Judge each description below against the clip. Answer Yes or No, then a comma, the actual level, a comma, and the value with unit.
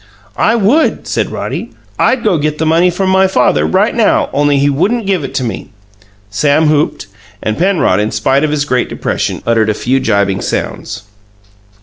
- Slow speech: No, average, 185 wpm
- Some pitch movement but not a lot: No, wide, 7.6 semitones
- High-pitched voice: No, medium, 145 Hz